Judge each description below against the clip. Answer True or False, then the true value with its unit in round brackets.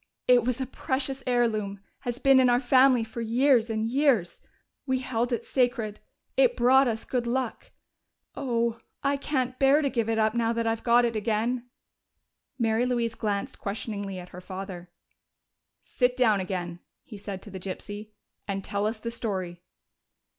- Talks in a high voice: True (230 Hz)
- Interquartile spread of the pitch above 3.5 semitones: False (3.2 semitones)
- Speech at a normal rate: True (170 wpm)